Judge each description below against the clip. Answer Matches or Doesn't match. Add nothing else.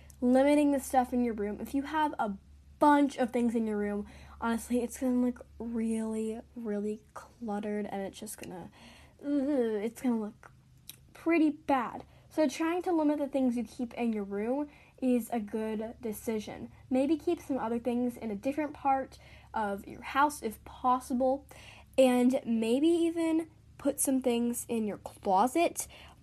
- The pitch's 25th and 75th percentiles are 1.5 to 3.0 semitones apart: Doesn't match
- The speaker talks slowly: Doesn't match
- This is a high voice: Matches